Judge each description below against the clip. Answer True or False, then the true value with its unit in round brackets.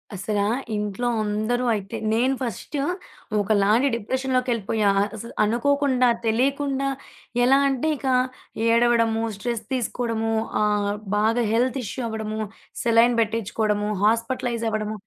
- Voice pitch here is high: True (230 Hz)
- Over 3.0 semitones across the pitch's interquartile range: False (2.7 semitones)